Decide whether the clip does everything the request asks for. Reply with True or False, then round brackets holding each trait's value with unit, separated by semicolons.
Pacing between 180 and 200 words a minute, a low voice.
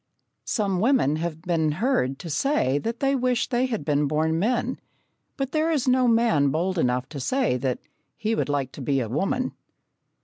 False (190 wpm; 180 Hz)